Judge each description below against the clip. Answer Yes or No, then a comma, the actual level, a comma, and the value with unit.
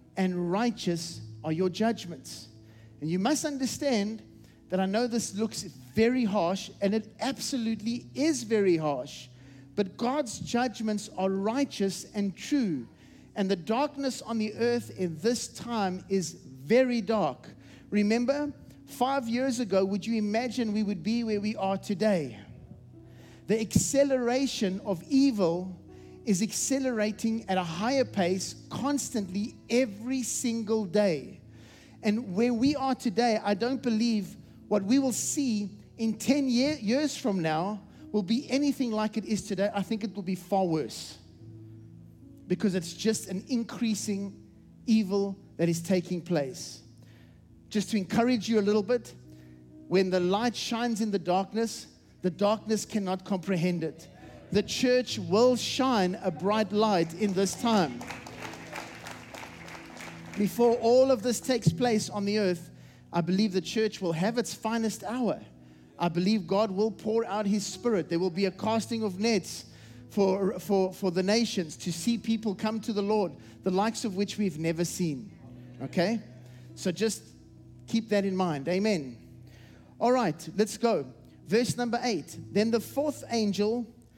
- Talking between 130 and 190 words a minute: Yes, average, 150 wpm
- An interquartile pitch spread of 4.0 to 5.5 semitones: Yes, average, 4.5 semitones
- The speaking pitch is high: Yes, high, 205 Hz